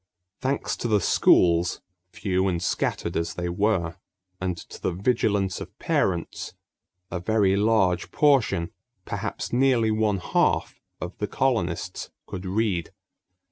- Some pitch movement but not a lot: Yes, average, 3.9 semitones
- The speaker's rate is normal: No, slow, 130 wpm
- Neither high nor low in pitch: No, very low, 95 Hz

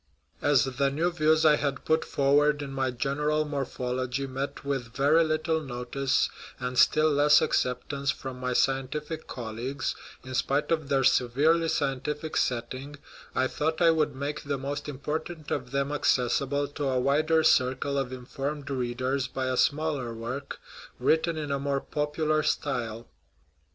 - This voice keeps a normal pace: Yes, average, 150 wpm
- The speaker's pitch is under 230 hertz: Yes, medium, 140 Hz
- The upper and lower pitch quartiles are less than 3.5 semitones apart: Yes, narrow, 2.6 semitones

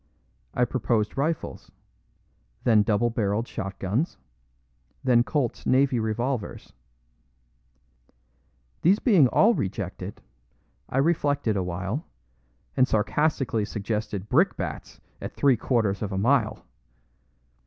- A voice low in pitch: Yes, low, 115 Hz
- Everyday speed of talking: No, slow, 95 wpm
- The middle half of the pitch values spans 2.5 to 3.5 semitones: No, average, 4.7 semitones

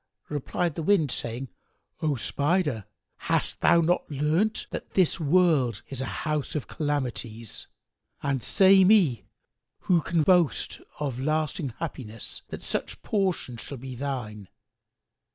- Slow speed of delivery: Yes, slow, 130 wpm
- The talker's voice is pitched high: No, medium, 145 Hz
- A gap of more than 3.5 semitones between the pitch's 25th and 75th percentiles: Yes, average, 5.0 semitones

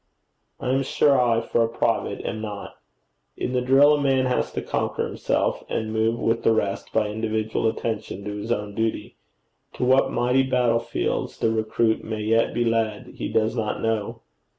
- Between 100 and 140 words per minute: No, average, 180 wpm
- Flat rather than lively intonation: Yes, narrow, 2.3 semitones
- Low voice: Yes, low, 115 Hz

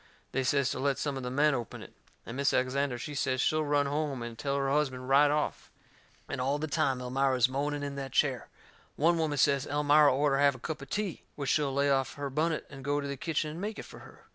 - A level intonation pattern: Yes, narrow, 1.8 semitones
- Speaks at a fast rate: Yes, fast, 250 wpm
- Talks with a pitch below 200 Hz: Yes, medium, 140 Hz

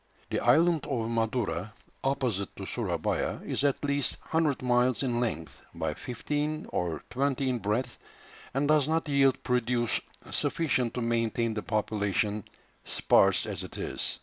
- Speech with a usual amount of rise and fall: Yes, average, 4.4 semitones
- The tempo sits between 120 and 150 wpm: Yes, average, 145 wpm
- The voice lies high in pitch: No, low, 125 Hz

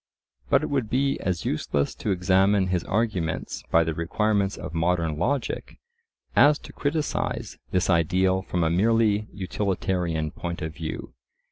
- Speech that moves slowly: No, average, 145 wpm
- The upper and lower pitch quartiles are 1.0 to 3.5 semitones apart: No, average, 4.2 semitones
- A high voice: No, very low, 95 Hz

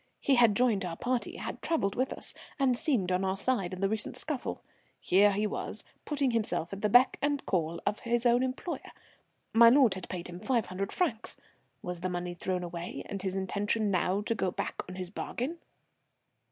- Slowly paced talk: No, average, 200 wpm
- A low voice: No, high, 205 Hz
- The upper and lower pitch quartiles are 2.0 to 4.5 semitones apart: No, average, 4.9 semitones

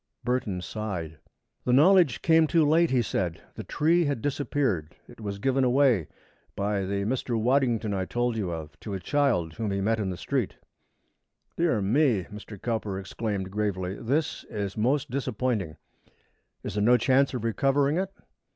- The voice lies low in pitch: Yes, low, 115 Hz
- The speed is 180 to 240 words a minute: No, average, 165 wpm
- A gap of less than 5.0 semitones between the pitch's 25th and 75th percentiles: No, wide, 5.6 semitones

